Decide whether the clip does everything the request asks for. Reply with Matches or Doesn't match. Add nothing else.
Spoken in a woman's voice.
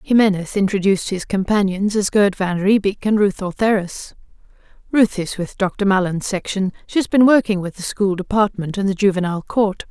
Matches